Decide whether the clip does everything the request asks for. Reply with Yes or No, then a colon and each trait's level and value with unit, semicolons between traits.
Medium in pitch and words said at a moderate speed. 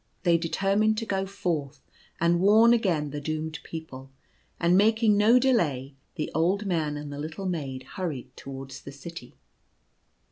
Yes: medium, 165 Hz; average, 150 wpm